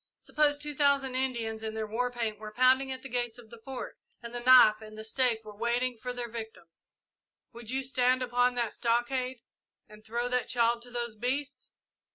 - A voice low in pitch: No, high, 245 Hz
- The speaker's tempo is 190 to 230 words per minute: Yes, average, 200 wpm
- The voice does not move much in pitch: Yes, narrow, 2.3 semitones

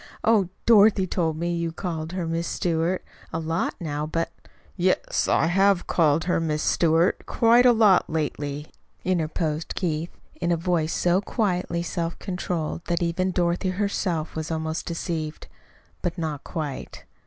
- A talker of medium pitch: Yes, medium, 170 Hz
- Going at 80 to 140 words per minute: No, average, 155 wpm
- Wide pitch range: No, narrow, 2.5 semitones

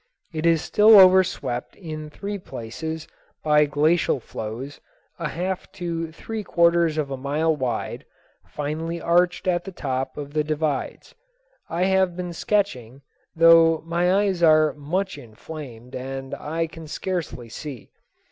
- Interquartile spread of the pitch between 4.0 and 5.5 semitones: No, average, 3.3 semitones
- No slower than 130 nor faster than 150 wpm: Yes, average, 140 wpm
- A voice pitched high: No, medium, 160 Hz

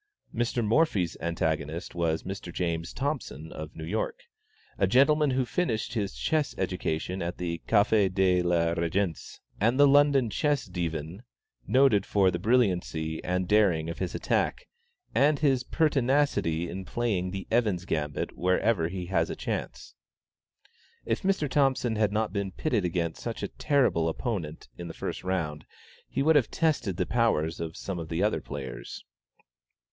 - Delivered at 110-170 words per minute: Yes, average, 155 wpm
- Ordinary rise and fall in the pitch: No, wide, 6.5 semitones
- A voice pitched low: Yes, very low, 95 Hz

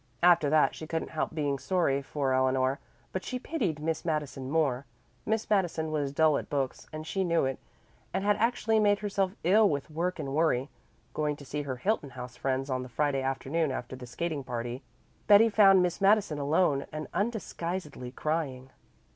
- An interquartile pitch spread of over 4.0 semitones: Yes, wide, 5.4 semitones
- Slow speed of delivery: No, average, 180 wpm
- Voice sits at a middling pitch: Yes, medium, 155 Hz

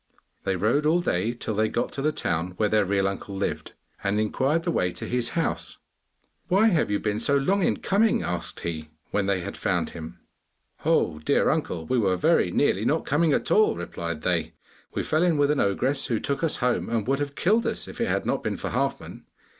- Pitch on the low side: Yes, low, 115 Hz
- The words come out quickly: Yes, fast, 220 wpm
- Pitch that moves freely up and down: Yes, wide, 7.7 semitones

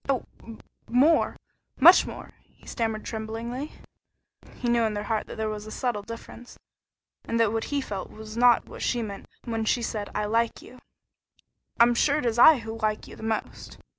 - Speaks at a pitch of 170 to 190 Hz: No, high, 230 Hz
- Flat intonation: Yes, narrow, 1.9 semitones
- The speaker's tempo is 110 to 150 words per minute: No, average, 190 wpm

